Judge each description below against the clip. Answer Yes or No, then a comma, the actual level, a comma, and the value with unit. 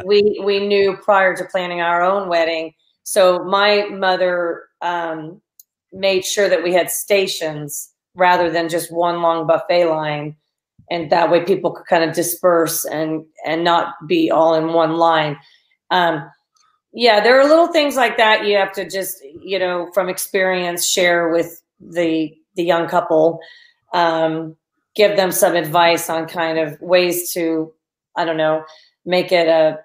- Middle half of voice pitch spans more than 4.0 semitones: No, average, 2.7 semitones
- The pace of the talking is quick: No, average, 160 wpm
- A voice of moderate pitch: Yes, medium, 175 Hz